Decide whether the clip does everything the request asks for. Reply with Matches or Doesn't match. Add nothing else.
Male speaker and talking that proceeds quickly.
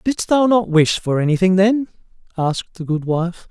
Doesn't match